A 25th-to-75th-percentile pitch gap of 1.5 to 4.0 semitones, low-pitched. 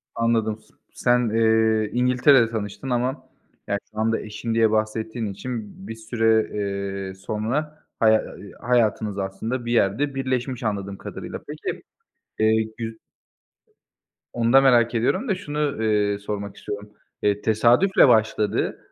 Yes: narrow, 2.6 semitones; low, 110 Hz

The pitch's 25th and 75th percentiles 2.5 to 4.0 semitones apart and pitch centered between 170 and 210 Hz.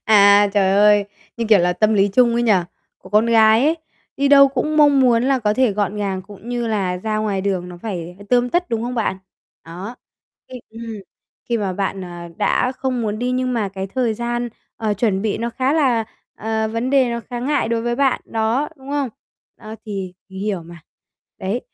No: average, 3.5 semitones; high, 225 Hz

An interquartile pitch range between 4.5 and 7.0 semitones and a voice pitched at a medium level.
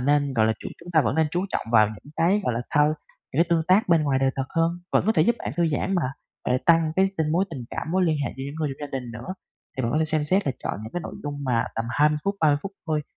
No: average, 4.1 semitones; medium, 155 Hz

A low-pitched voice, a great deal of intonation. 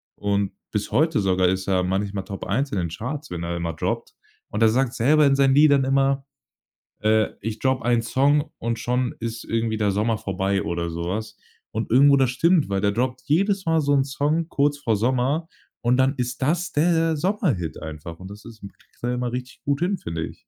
Yes: low, 120 Hz; wide, 5.9 semitones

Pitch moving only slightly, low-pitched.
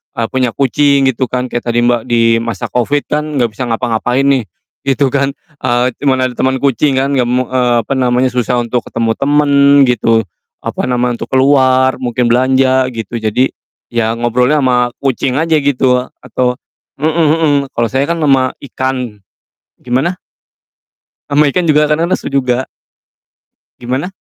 Yes: narrow, 2.3 semitones; low, 130 Hz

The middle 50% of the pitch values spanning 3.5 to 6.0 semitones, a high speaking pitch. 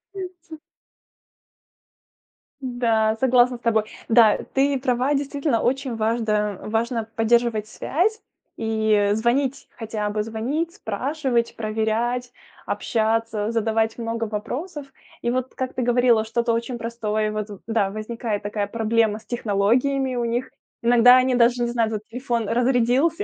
No: narrow, 2.4 semitones; high, 235 Hz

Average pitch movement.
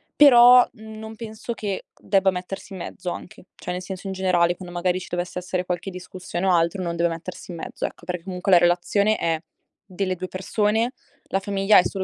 No: narrow, 2.2 semitones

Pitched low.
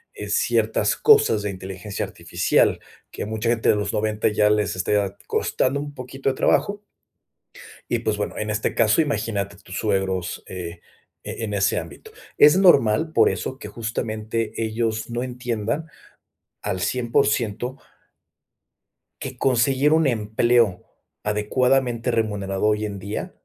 Yes: low, 110 Hz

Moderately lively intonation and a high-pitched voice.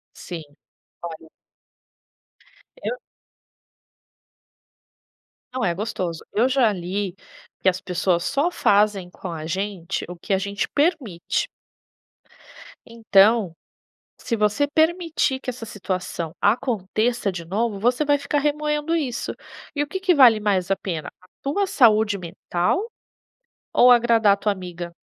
No: wide, 6.5 semitones; high, 210 Hz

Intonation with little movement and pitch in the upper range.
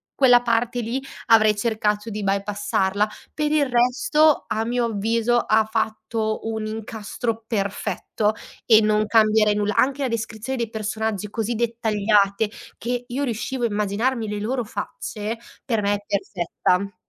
Yes: narrow, 2.3 semitones; high, 220 Hz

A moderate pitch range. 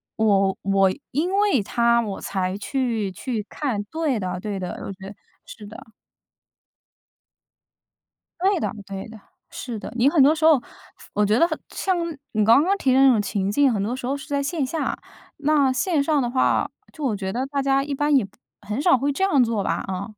No: wide, 5.7 semitones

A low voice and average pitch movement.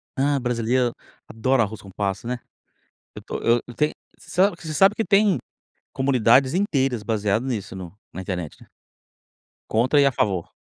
Yes: low, 120 Hz; average, 4.8 semitones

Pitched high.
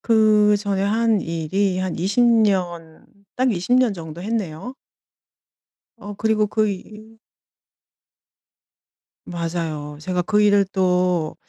Yes: high, 200 Hz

